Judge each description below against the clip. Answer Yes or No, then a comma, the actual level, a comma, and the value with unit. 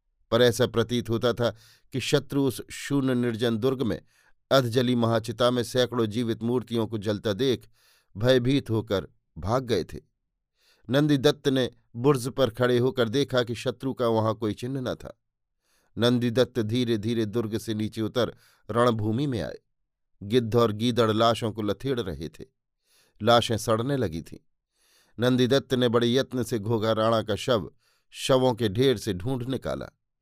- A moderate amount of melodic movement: No, narrow, 2.3 semitones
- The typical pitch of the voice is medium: No, low, 120 Hz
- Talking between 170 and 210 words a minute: No, average, 155 wpm